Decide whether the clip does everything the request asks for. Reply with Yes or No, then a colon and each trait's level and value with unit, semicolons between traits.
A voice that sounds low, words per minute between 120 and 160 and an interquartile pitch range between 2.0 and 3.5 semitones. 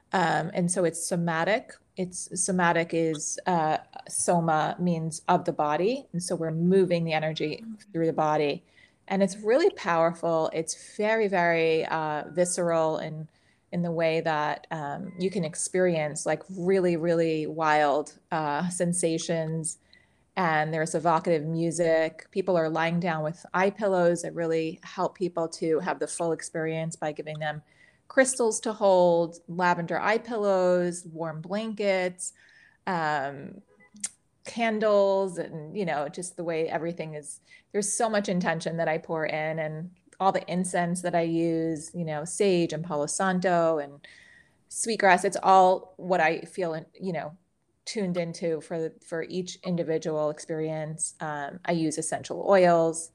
No: medium, 170 Hz; average, 150 wpm; narrow, 2.5 semitones